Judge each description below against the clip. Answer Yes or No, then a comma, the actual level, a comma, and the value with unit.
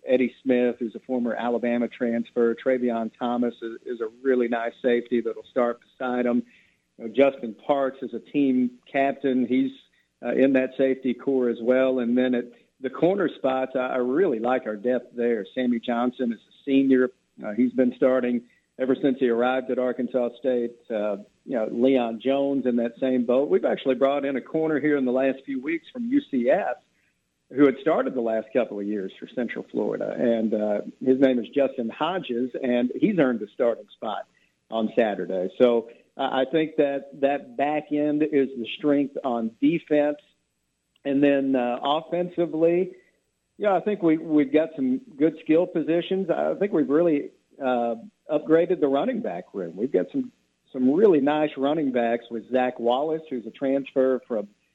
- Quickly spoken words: No, average, 180 wpm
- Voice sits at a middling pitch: No, low, 130 Hz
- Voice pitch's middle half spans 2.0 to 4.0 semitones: Yes, average, 3.1 semitones